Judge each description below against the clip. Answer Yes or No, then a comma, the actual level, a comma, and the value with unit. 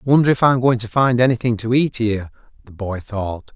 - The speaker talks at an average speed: No, fast, 220 wpm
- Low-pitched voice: Yes, low, 115 Hz